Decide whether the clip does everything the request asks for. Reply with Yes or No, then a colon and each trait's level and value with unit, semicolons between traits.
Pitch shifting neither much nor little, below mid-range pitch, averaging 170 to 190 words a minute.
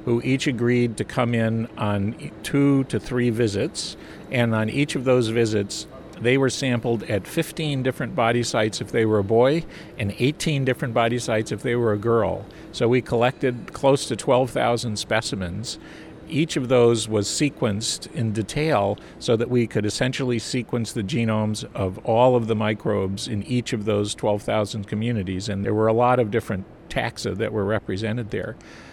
Yes: average, 3.1 semitones; low, 115 Hz; average, 175 wpm